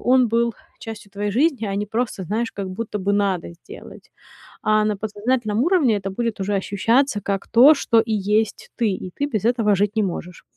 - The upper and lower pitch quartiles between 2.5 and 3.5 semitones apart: Yes, average, 2.8 semitones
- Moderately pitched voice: No, high, 215 Hz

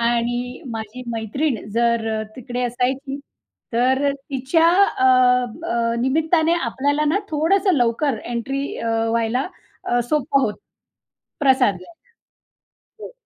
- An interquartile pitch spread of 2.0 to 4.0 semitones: Yes, average, 3.6 semitones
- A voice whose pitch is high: Yes, very high, 255 Hz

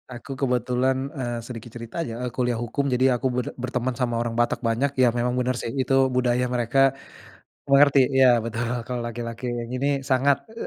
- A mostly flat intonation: Yes, narrow, 1.8 semitones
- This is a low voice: Yes, low, 125 Hz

